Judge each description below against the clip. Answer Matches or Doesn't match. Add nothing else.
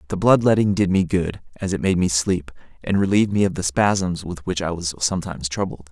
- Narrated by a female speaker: Doesn't match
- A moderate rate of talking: Doesn't match